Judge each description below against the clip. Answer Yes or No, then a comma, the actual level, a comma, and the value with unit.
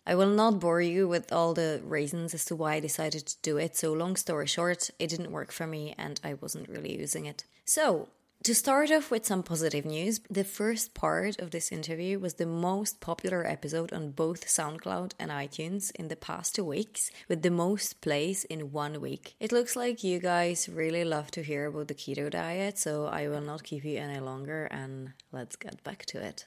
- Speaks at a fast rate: Yes, fast, 215 wpm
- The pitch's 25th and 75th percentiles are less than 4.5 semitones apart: Yes, average, 3.7 semitones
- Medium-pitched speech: Yes, medium, 165 Hz